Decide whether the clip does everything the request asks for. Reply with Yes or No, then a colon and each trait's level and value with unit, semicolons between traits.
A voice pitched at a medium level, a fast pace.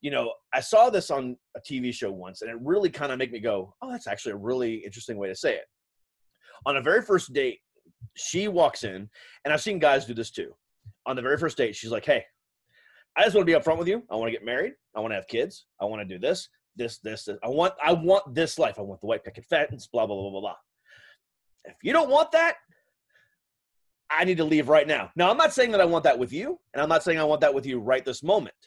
Yes: medium, 150 Hz; fast, 270 wpm